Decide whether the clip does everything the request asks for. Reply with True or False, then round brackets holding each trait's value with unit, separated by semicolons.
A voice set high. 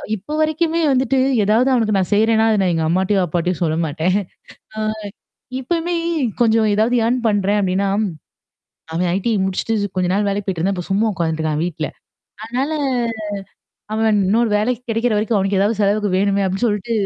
True (205 Hz)